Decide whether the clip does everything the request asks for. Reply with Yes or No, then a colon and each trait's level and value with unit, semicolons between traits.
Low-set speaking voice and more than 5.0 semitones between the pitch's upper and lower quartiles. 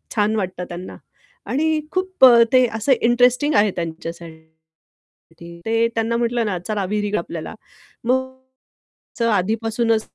No: high, 220 Hz; wide, 5.5 semitones